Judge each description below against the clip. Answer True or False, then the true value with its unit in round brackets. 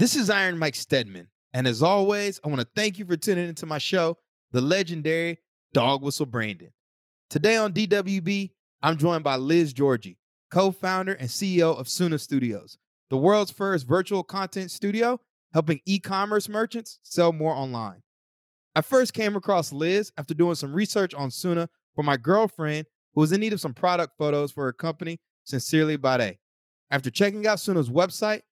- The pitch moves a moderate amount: False (5.9 semitones)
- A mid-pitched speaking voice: True (165 Hz)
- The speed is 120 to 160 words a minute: False (170 wpm)